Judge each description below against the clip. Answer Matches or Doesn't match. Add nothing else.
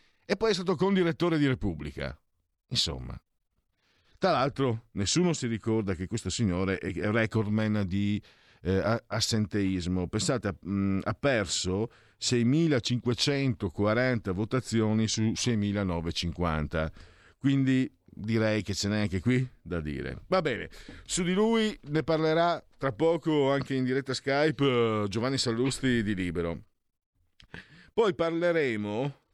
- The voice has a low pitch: Matches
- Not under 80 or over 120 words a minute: Matches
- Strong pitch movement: Matches